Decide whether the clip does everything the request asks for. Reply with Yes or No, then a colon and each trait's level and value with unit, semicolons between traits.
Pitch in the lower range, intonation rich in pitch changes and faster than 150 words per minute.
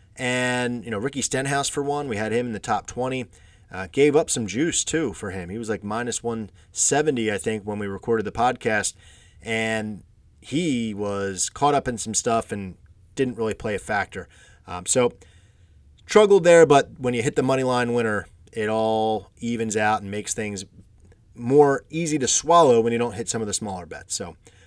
No: low, 110 Hz; average, 4.1 semitones; average, 200 wpm